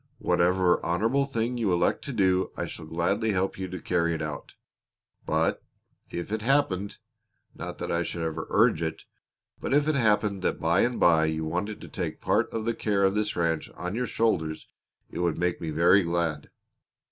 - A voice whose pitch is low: Yes, very low, 90 Hz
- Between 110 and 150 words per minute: No, average, 190 wpm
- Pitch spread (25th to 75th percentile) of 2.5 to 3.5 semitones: No, average, 4.4 semitones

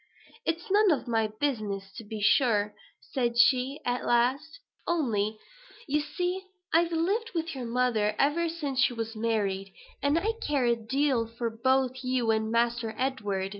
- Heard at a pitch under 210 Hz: No, very high, 250 Hz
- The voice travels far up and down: No, average, 4.9 semitones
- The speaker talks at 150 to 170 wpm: Yes, average, 160 wpm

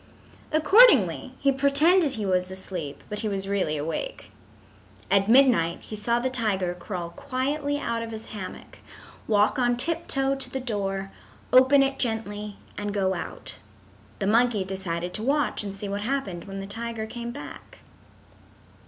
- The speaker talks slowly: No, average, 160 wpm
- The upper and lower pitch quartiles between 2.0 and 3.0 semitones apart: No, wide, 5.4 semitones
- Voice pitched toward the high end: Yes, high, 220 Hz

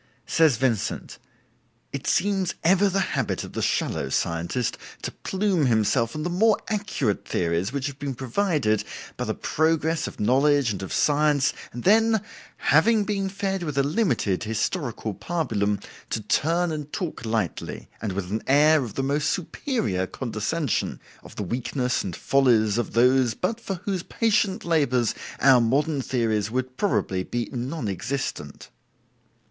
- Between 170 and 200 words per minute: No, average, 155 wpm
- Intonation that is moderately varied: No, wide, 7.3 semitones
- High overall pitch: No, medium, 140 Hz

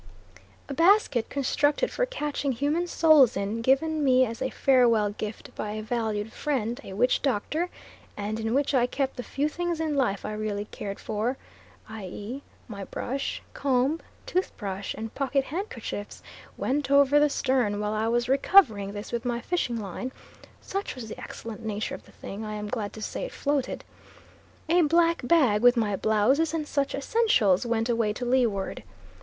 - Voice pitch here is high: Yes, high, 245 Hz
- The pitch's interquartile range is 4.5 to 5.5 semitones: Yes, average, 5.2 semitones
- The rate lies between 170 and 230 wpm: Yes, average, 175 wpm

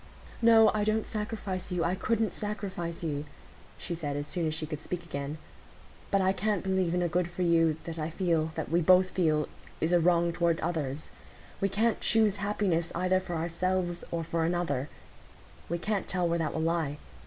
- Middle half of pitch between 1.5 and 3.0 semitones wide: Yes, narrow, 2.6 semitones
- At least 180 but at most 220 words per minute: Yes, average, 190 wpm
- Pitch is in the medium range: Yes, medium, 175 Hz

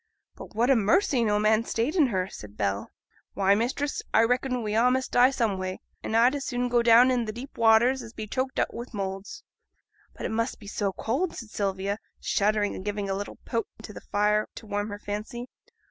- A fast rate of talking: Yes, fast, 220 wpm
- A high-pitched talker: Yes, high, 220 Hz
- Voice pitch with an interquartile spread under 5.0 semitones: Yes, average, 3.2 semitones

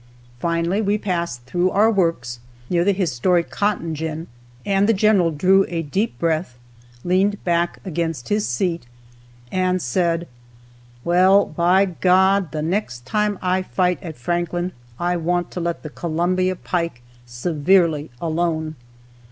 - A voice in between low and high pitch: Yes, medium, 175 Hz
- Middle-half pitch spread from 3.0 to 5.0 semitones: No, narrow, 2.6 semitones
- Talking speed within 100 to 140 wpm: Yes, slow, 135 wpm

